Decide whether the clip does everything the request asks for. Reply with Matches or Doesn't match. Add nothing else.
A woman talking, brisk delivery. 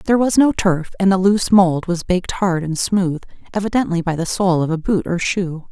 Matches